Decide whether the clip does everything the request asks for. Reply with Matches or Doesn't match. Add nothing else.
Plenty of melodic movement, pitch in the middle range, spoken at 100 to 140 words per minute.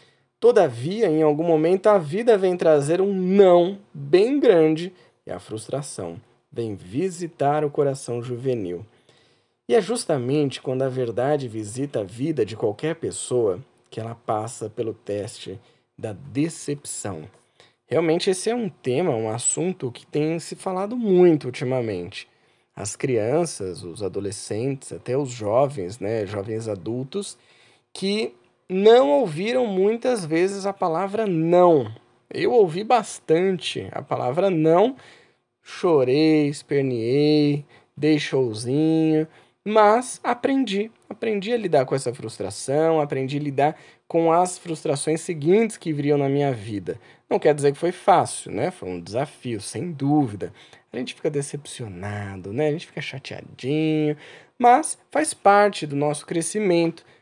Matches